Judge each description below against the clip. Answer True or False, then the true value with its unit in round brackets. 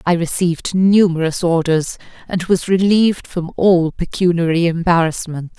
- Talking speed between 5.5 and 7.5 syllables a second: False (4.6 syllables/s)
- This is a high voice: False (175 Hz)